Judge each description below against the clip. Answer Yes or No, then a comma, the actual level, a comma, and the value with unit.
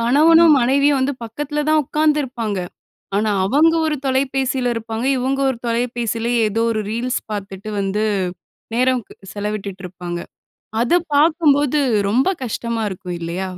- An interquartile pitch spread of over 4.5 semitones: Yes, average, 5.0 semitones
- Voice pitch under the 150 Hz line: No, high, 245 Hz